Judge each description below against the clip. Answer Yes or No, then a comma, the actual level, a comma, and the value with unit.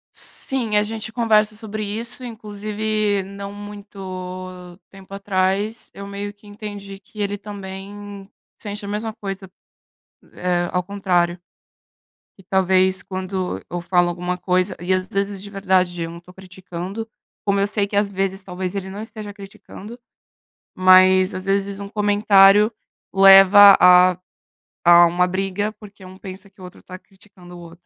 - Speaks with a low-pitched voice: No, high, 195 Hz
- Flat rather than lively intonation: Yes, narrow, 1.8 semitones